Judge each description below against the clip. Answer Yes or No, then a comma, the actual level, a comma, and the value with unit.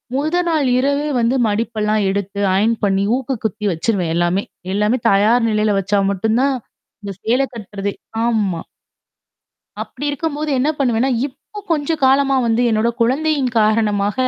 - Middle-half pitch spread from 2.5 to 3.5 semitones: No, average, 4.7 semitones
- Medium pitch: No, high, 225 Hz